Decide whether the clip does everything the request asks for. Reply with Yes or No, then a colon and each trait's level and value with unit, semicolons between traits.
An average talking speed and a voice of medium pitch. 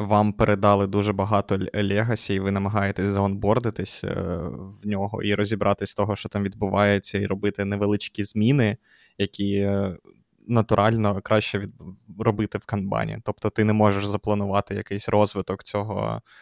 No: average, 130 wpm; low, 100 Hz